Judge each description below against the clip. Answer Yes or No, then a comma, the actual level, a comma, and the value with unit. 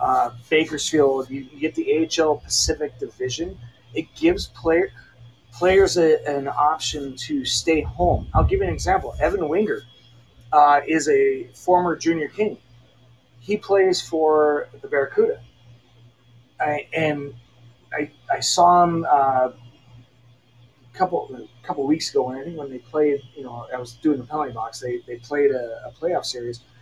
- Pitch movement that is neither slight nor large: Yes, average, 4.6 semitones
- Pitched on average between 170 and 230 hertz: No, medium, 140 Hz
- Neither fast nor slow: Yes, average, 155 wpm